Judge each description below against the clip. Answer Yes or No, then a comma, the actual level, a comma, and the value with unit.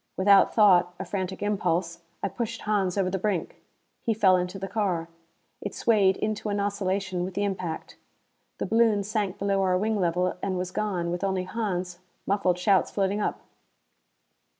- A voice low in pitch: No, high, 195 Hz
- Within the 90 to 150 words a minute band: No, average, 170 wpm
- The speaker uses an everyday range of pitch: No, narrow, 2.1 semitones